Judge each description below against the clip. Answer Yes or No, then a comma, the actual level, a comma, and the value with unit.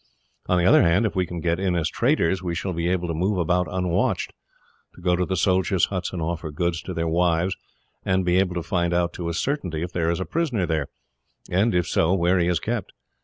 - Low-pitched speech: Yes, very low, 90 Hz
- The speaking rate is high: Yes, fast, 240 wpm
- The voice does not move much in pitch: Yes, narrow, 1.7 semitones